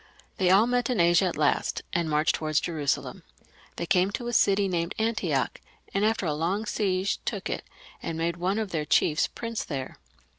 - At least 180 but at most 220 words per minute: Yes, average, 190 wpm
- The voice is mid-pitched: Yes, medium, 180 Hz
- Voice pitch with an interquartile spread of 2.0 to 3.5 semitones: No, average, 4.4 semitones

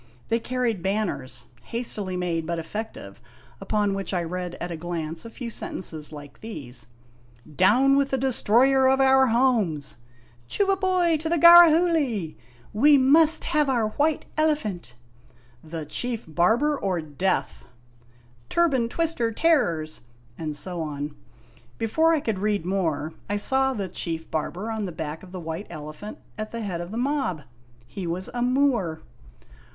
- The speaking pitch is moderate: No, high, 200 Hz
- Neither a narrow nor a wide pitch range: No, wide, 8.6 semitones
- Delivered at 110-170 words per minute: Yes, average, 165 wpm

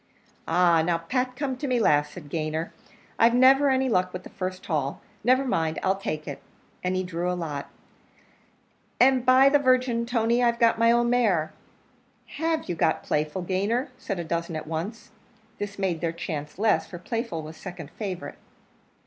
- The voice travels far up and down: Yes, wide, 6.7 semitones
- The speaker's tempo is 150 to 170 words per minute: No, average, 180 wpm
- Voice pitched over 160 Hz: Yes, high, 190 Hz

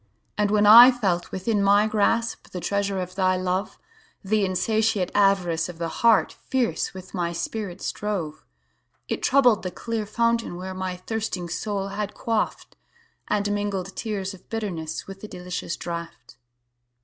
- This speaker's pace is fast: No, average, 140 wpm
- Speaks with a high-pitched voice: Yes, high, 200 Hz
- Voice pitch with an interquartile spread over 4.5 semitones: No, average, 3.2 semitones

